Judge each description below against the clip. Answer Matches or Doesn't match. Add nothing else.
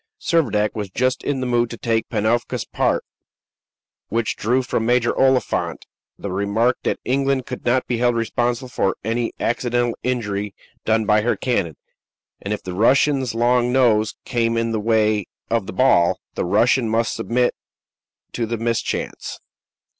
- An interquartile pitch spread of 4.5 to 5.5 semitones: Doesn't match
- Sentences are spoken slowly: Doesn't match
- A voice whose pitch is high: Doesn't match